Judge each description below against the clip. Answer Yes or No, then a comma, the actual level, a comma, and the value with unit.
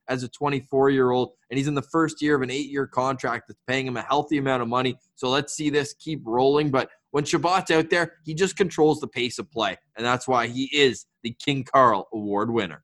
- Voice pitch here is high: No, low, 135 Hz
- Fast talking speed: Yes, fast, 245 wpm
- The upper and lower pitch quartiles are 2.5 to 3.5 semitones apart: Yes, average, 2.9 semitones